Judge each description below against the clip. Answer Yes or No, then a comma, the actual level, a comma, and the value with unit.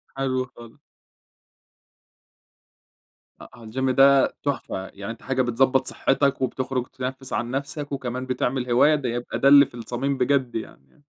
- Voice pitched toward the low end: Yes, low, 130 Hz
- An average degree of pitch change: No, narrow, 1.9 semitones